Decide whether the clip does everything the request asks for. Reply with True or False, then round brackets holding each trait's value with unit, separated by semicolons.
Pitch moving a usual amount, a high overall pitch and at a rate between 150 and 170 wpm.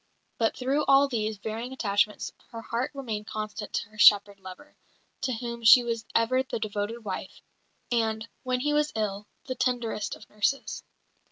True (3.1 semitones; 225 Hz; 165 wpm)